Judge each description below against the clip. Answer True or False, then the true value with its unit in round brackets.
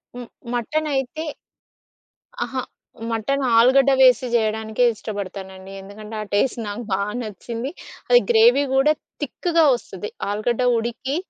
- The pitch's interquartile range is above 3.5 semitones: True (4.3 semitones)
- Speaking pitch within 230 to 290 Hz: True (235 Hz)